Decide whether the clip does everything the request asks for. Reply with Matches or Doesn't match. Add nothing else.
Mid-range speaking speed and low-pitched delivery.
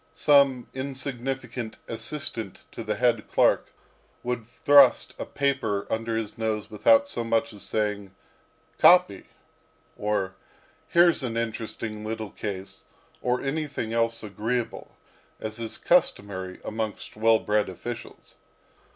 Doesn't match